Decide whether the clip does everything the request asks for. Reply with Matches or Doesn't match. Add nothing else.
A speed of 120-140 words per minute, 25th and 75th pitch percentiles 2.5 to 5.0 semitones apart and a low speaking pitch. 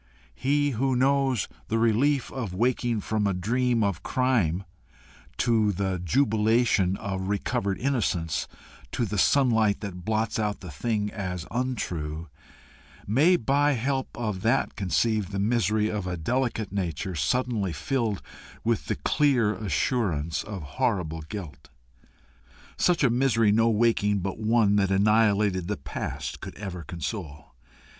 Matches